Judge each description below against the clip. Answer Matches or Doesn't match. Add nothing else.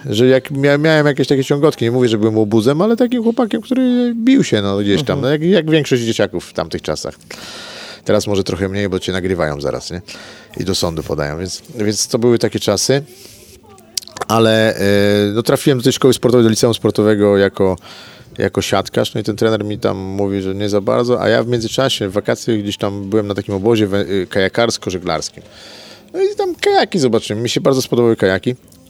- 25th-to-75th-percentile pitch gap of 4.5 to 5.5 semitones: Matches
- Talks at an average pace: Doesn't match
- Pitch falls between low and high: Doesn't match